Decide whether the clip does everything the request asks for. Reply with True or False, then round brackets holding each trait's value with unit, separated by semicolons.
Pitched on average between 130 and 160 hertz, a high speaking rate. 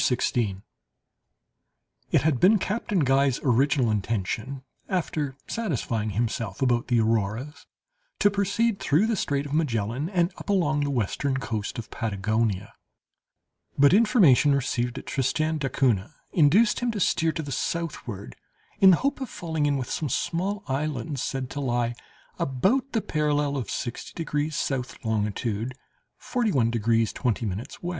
False (140 Hz; 145 wpm)